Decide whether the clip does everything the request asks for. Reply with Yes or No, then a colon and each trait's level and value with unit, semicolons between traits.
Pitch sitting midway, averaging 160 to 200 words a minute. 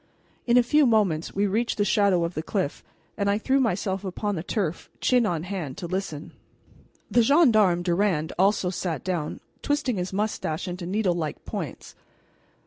No: high, 195 Hz; average, 165 wpm